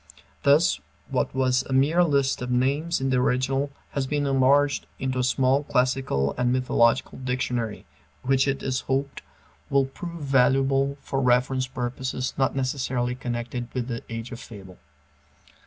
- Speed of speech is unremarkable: Yes, average, 150 wpm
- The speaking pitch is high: No, low, 130 Hz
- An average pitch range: No, narrow, 1.7 semitones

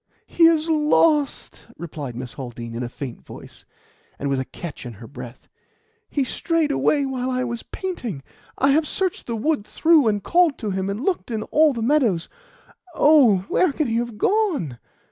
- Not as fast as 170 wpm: No, average, 185 wpm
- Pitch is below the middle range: No, high, 240 Hz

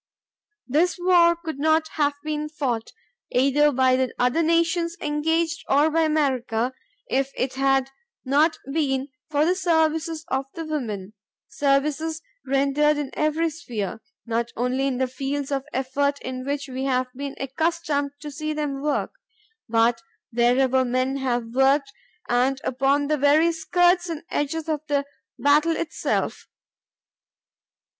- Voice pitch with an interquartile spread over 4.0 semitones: No, average, 3.2 semitones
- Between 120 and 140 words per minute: Yes, slow, 135 wpm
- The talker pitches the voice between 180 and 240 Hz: No, very high, 285 Hz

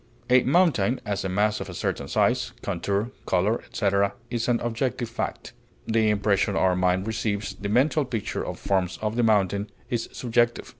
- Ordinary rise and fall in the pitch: Yes, average, 3.1 semitones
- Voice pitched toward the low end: Yes, low, 105 Hz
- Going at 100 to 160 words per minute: No, average, 170 wpm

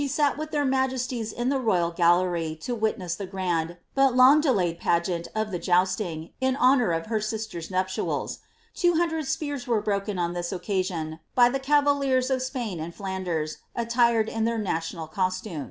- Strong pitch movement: Yes, wide, 6.7 semitones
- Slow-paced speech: No, average, 170 wpm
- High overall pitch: Yes, high, 215 Hz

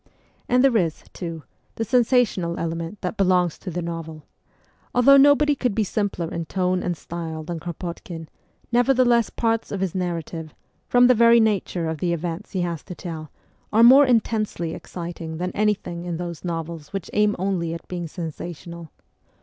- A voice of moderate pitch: Yes, medium, 180 Hz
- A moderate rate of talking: Yes, average, 165 wpm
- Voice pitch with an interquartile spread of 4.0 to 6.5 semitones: Yes, average, 4.6 semitones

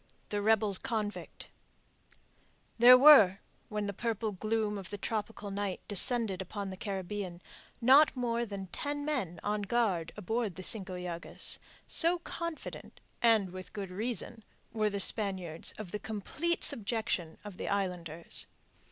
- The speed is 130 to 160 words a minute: Yes, average, 140 wpm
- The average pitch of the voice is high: Yes, high, 205 Hz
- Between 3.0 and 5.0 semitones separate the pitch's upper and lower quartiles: Yes, average, 3.4 semitones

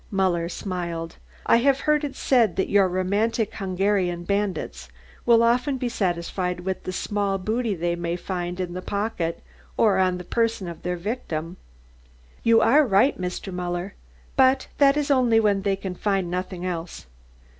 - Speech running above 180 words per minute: No, average, 165 wpm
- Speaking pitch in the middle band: No, high, 195 Hz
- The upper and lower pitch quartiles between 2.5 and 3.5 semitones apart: No, average, 4.1 semitones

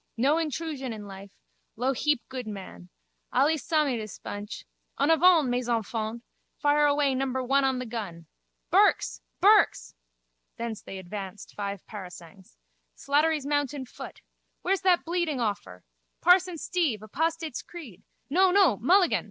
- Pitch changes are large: Yes, wide, 6.7 semitones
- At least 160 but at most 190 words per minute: No, slow, 135 wpm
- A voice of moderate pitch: No, very high, 260 Hz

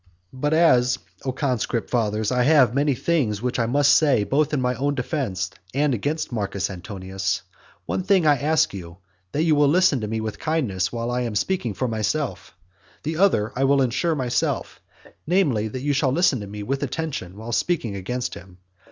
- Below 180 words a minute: No, average, 195 wpm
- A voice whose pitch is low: Yes, low, 125 Hz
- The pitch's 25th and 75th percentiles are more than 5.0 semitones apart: Yes, wide, 5.5 semitones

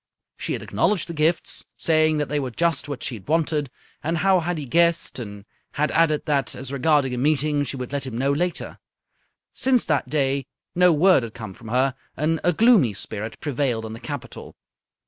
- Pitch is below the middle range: No, medium, 145 Hz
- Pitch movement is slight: No, average, 4.2 semitones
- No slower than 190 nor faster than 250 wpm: Yes, average, 200 wpm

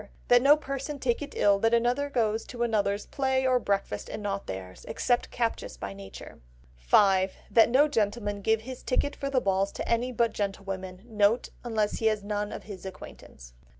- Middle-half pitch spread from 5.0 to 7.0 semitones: No, average, 3.8 semitones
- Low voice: No, high, 220 Hz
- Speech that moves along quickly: No, average, 185 wpm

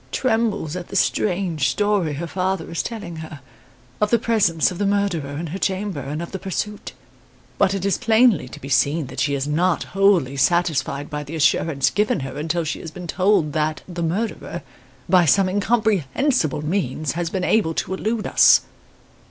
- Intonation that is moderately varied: Yes, average, 4.7 semitones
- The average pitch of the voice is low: No, medium, 175 Hz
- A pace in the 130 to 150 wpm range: No, average, 185 wpm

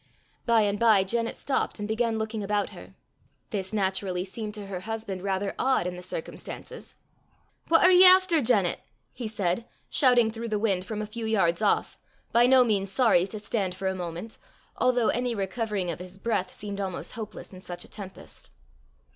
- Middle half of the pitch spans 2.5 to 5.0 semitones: Yes, average, 3.4 semitones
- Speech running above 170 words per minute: Yes, average, 185 wpm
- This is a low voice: No, high, 210 Hz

